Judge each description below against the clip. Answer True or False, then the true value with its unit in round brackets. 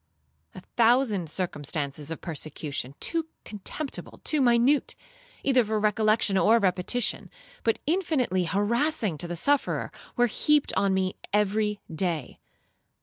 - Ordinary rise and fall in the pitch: False (5.7 semitones)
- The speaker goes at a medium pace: False (120 wpm)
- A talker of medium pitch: False (210 Hz)